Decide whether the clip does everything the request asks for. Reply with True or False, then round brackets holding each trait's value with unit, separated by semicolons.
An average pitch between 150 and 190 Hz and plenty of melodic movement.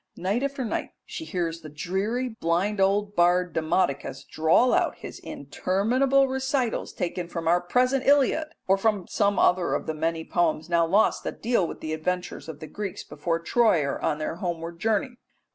True (185 Hz; 5.7 semitones)